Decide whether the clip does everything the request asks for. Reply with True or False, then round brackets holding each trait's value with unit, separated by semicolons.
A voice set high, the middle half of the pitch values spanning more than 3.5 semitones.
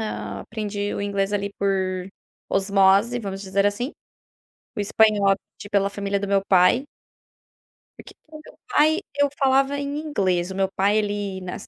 False (200 Hz; 2.4 semitones)